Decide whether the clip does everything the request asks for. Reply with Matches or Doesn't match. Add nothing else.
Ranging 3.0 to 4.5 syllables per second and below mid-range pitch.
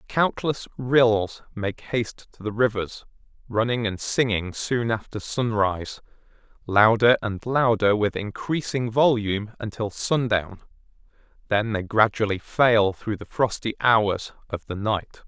Matches